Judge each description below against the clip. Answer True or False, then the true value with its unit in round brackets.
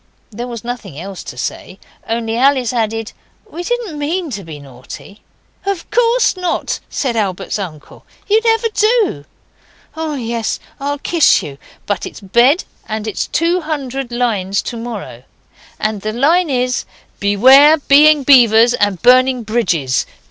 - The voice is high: True (245 Hz)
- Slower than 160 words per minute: True (150 wpm)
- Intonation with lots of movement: True (6.6 semitones)